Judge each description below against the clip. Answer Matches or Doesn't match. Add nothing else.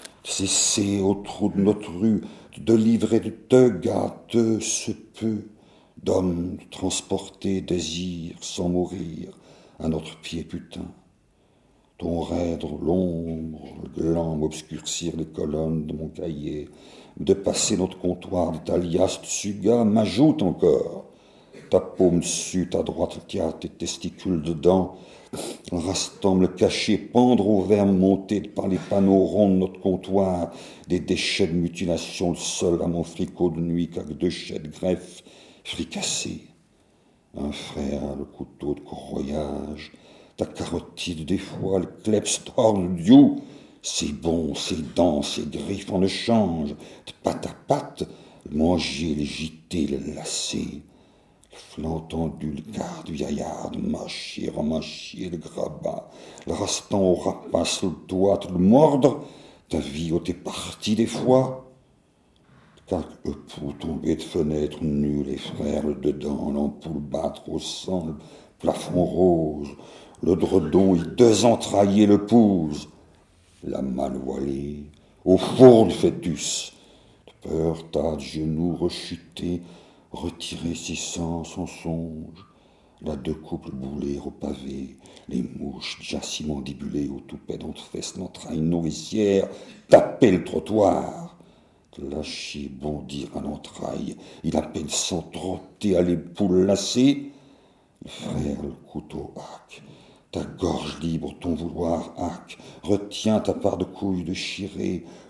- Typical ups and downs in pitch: Matches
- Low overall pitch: Matches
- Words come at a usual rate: Doesn't match